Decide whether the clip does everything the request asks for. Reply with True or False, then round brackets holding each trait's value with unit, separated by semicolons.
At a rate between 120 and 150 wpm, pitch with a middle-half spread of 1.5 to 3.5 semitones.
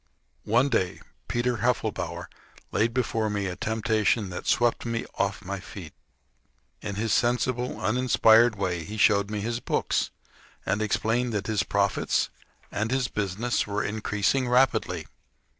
True (140 wpm; 3.0 semitones)